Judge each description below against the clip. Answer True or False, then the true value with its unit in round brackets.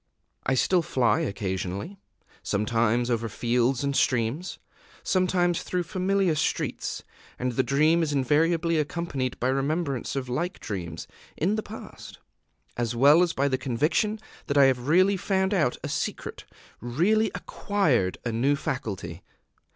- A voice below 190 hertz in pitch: True (140 Hz)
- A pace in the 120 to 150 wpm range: True (140 wpm)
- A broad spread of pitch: True (6.3 semitones)